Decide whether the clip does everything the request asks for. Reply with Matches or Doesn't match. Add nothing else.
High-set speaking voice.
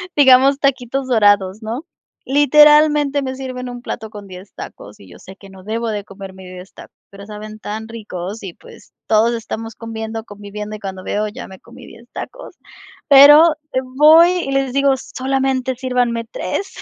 Matches